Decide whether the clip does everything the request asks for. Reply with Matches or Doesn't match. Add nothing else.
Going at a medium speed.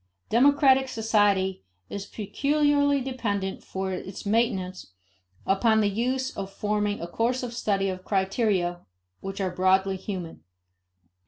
Doesn't match